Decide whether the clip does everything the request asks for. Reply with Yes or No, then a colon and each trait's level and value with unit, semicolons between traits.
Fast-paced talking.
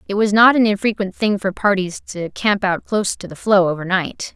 Yes: fast, 235 wpm